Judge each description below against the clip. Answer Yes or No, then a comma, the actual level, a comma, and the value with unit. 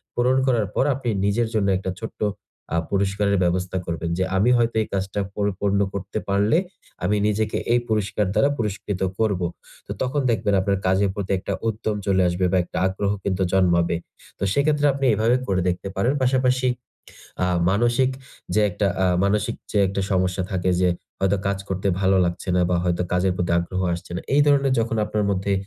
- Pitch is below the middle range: Yes, low, 100 Hz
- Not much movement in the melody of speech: No, average, 3.1 semitones